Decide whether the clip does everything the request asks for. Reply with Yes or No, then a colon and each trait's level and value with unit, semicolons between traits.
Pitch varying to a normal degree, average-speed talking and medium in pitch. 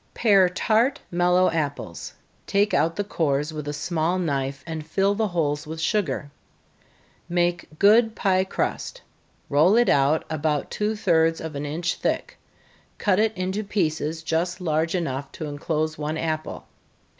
Yes: average, 3.6 semitones; average, 155 wpm; medium, 165 Hz